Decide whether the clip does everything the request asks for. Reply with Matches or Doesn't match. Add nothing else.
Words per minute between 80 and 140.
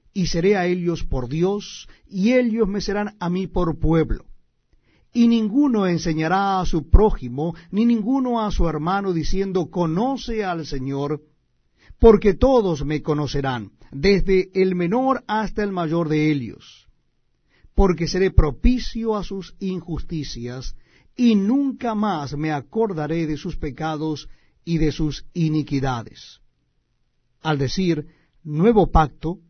Matches